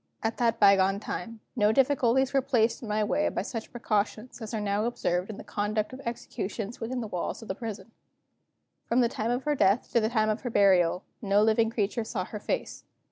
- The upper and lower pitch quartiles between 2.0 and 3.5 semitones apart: Yes, narrow, 2.6 semitones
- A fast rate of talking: Yes, fast, 215 wpm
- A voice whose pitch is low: No, high, 220 Hz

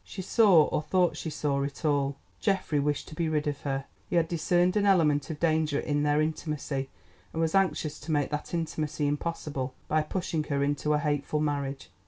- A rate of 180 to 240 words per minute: Yes, average, 200 wpm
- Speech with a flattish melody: Yes, narrow, 2.3 semitones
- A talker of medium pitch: Yes, medium, 150 Hz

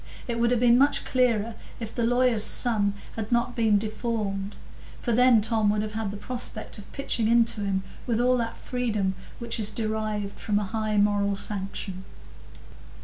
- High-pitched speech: Yes, high, 220 Hz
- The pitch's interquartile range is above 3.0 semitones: No, narrow, 2.4 semitones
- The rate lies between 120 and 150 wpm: No, average, 175 wpm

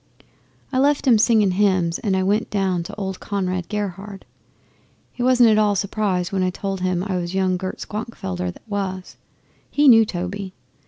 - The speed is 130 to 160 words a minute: No, average, 175 wpm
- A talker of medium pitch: No, high, 195 Hz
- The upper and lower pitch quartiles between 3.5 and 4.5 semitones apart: No, narrow, 2.4 semitones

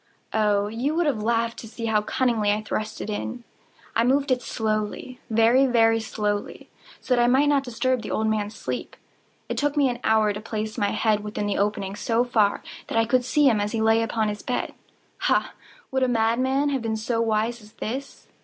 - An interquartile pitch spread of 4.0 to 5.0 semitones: No, average, 2.7 semitones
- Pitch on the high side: Yes, high, 225 Hz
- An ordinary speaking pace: No, fast, 210 wpm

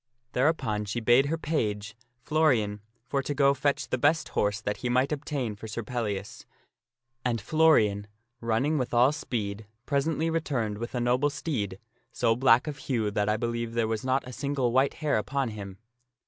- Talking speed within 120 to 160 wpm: No, average, 175 wpm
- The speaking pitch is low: Yes, low, 120 Hz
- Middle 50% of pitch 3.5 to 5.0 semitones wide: Yes, average, 4.7 semitones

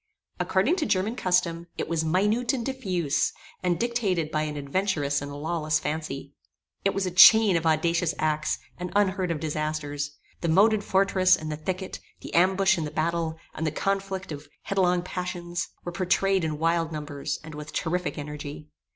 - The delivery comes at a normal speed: Yes, average, 170 wpm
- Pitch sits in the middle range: Yes, medium, 170 Hz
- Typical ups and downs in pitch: Yes, average, 3.6 semitones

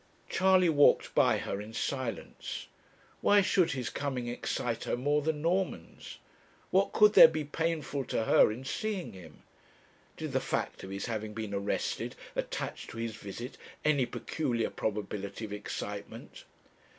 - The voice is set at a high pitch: No, low, 125 Hz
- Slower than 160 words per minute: Yes, average, 150 wpm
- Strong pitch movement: Yes, wide, 6.6 semitones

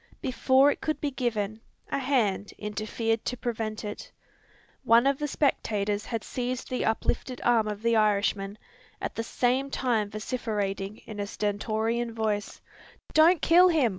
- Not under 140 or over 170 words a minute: Yes, average, 150 wpm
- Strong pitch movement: No, average, 3.4 semitones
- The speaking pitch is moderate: No, high, 225 Hz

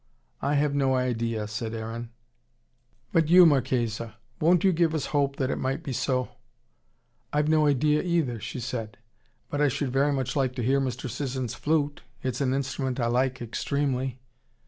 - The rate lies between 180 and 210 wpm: No, average, 170 wpm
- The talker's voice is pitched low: Yes, low, 130 Hz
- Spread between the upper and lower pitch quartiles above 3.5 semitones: No, average, 3.1 semitones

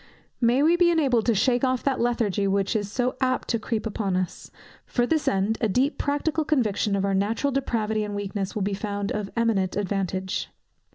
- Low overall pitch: No, high, 220 Hz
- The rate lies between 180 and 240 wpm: Yes, average, 195 wpm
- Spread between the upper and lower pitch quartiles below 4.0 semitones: No, average, 4.3 semitones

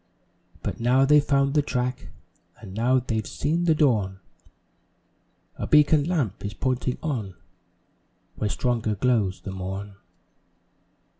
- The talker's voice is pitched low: Yes, low, 125 Hz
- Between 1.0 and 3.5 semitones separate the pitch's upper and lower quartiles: No, wide, 5.6 semitones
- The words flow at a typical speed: No, slow, 125 wpm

